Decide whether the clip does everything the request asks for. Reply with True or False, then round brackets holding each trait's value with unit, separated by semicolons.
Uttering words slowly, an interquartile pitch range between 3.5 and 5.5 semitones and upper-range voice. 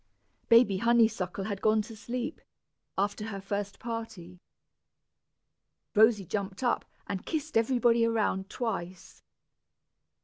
False (105 wpm; 3.0 semitones; 215 Hz)